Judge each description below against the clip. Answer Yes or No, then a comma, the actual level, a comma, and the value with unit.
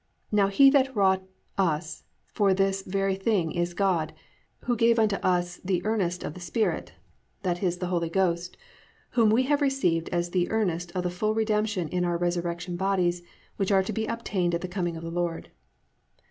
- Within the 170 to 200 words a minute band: Yes, average, 185 wpm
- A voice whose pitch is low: No, medium, 185 Hz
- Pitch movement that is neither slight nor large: Yes, average, 3.3 semitones